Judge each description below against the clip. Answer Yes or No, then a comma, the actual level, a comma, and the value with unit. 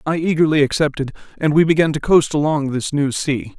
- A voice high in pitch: No, medium, 150 Hz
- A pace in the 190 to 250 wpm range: Yes, average, 200 wpm